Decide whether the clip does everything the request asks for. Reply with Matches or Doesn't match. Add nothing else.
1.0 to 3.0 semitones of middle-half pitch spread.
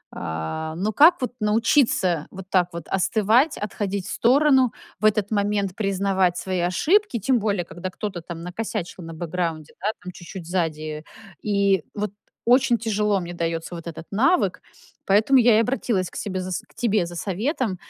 Doesn't match